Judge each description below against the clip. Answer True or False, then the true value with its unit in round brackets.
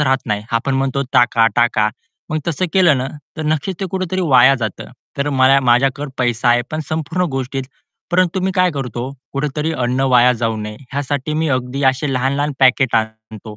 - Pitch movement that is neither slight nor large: True (3.7 semitones)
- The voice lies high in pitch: False (135 Hz)